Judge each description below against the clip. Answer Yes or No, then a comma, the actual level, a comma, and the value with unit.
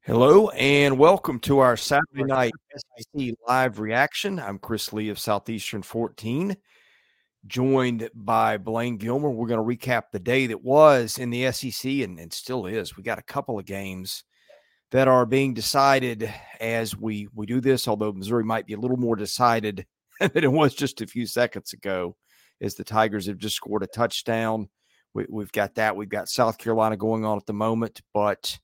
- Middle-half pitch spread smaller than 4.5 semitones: Yes, average, 3.3 semitones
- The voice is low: Yes, low, 115 Hz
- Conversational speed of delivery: Yes, average, 185 wpm